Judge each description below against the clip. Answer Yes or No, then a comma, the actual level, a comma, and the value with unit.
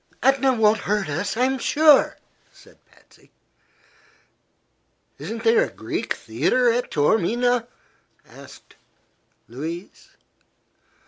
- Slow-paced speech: Yes, slow, 90 wpm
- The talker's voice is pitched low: No, high, 225 Hz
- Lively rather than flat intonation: Yes, wide, 6.4 semitones